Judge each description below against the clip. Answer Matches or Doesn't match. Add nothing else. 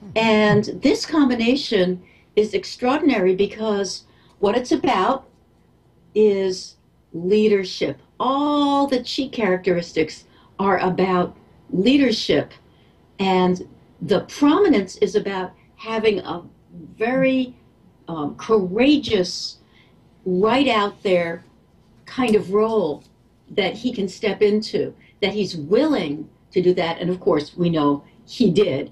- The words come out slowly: Matches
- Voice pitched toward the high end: Matches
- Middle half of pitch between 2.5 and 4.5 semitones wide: Doesn't match